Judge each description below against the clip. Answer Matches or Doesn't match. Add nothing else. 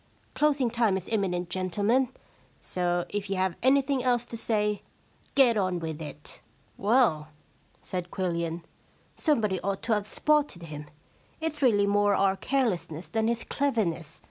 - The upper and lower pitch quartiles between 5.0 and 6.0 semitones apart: Matches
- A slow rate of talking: Doesn't match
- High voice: Matches